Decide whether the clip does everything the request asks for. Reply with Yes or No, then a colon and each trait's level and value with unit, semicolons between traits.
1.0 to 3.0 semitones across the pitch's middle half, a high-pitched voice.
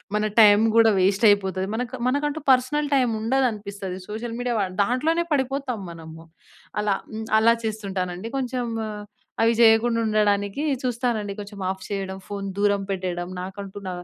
No: average, 3.8 semitones; high, 215 Hz